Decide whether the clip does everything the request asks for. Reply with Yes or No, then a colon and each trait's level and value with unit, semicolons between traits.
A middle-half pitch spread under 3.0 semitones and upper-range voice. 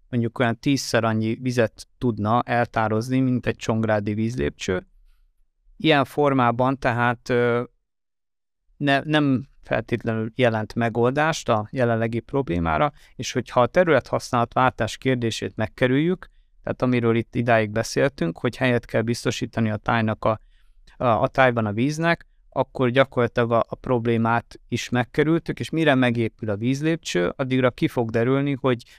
No: narrow, 2.5 semitones; low, 120 Hz